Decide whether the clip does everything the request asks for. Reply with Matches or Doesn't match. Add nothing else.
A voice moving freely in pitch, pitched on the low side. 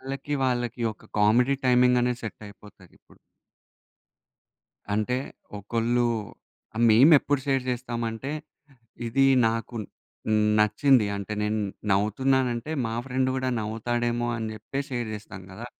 Doesn't match